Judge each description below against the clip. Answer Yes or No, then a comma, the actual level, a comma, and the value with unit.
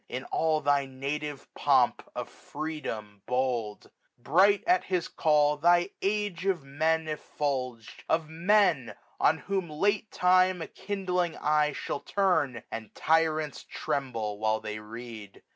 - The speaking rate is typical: No, slow, 130 wpm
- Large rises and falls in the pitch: Yes, wide, 5.8 semitones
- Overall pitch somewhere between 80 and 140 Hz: No, medium, 150 Hz